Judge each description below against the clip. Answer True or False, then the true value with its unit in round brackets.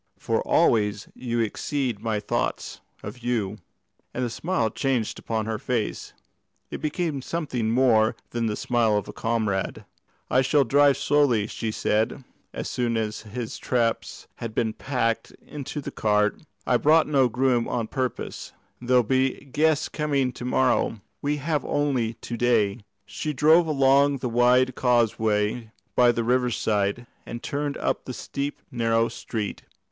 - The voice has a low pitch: True (120 Hz)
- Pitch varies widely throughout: False (3.5 semitones)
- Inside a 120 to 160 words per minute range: True (150 wpm)